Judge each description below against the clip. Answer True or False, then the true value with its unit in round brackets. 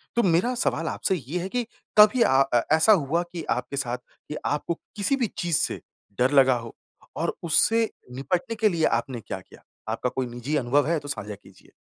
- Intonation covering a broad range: True (6.6 semitones)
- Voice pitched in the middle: True (150 Hz)